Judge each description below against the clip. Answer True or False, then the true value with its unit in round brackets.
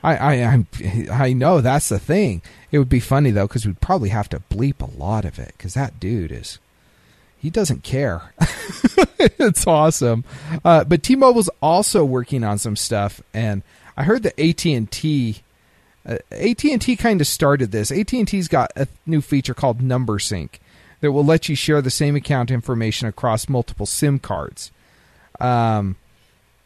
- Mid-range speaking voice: False (130 Hz)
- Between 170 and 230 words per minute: False (160 wpm)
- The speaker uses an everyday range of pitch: False (6.0 semitones)